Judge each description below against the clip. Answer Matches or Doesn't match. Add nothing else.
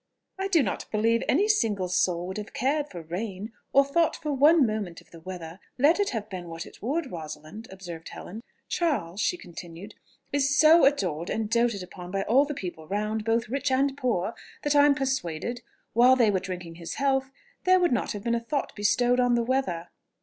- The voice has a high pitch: Matches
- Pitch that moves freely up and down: Matches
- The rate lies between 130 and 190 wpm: Doesn't match